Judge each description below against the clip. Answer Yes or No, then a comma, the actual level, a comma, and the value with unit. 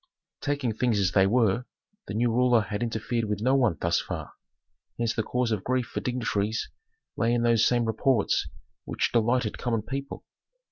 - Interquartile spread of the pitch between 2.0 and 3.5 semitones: Yes, narrow, 2.5 semitones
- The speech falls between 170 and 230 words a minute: Yes, average, 175 wpm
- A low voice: Yes, low, 115 Hz